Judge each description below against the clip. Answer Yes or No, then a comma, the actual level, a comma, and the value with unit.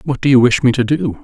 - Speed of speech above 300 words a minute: Yes, fast, 340 wpm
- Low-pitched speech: Yes, low, 130 Hz